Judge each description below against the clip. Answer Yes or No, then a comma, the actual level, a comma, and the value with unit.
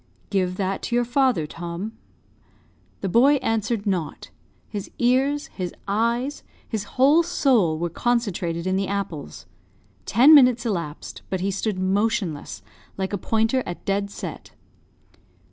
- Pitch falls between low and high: No, high, 205 Hz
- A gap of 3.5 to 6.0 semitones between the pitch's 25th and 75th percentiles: Yes, average, 4.8 semitones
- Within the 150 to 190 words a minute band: No, slow, 135 wpm